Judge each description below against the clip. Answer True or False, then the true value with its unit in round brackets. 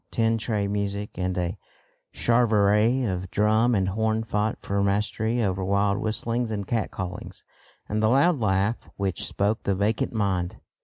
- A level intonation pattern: True (2.2 semitones)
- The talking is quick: False (155 wpm)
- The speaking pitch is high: False (105 Hz)